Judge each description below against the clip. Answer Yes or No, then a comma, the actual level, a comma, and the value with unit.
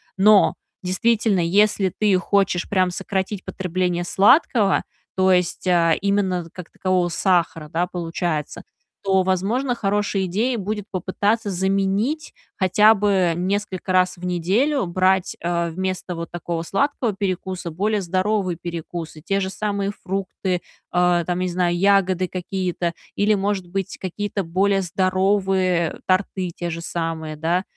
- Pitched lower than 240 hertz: Yes, medium, 185 Hz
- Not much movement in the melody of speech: Yes, narrow, 2.3 semitones